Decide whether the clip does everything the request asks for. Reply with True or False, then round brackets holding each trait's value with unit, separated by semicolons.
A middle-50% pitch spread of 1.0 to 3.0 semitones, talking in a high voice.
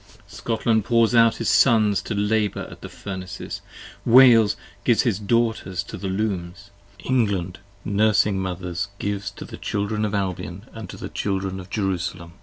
False (2.7 semitones; 100 Hz)